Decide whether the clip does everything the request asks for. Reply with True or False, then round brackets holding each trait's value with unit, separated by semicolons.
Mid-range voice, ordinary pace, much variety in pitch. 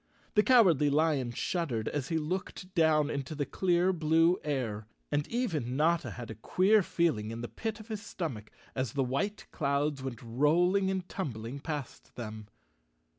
True (150 Hz; 165 wpm; 5.9 semitones)